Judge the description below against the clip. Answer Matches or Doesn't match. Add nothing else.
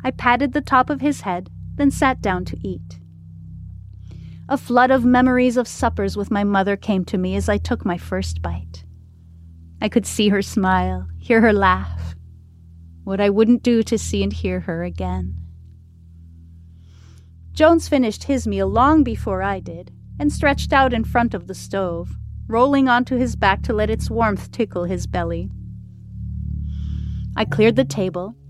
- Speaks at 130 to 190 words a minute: Matches